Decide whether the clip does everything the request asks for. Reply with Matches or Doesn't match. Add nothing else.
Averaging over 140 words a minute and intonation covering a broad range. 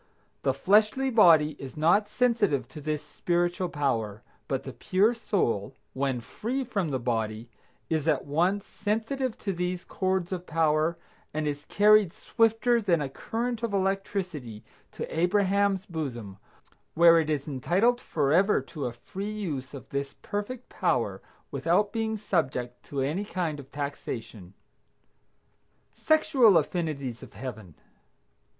Doesn't match